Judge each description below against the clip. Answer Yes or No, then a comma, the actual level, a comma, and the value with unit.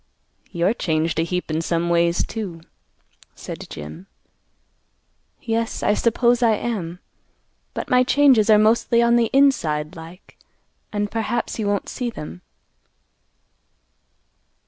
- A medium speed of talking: No, slow, 125 wpm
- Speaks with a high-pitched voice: Yes, high, 205 Hz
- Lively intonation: Yes, wide, 5.7 semitones